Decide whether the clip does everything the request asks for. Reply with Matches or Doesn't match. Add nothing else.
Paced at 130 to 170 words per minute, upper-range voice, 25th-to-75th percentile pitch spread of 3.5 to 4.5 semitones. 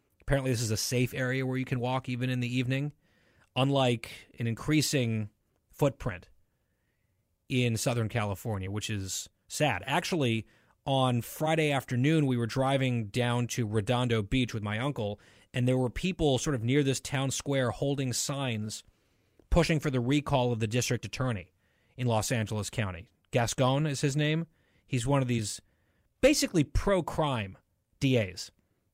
Doesn't match